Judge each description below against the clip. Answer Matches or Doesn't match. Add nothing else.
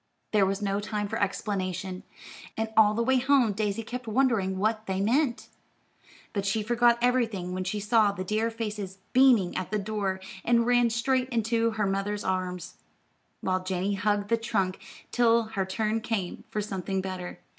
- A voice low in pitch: Doesn't match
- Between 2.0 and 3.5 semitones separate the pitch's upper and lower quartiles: Matches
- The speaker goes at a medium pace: Matches